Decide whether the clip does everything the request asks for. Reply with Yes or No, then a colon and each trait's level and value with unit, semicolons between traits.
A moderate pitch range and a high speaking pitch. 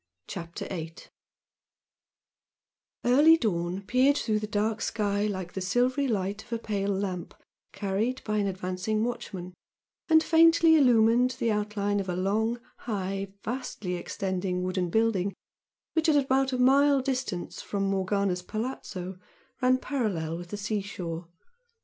Yes: average, 4.9 semitones; high, 210 Hz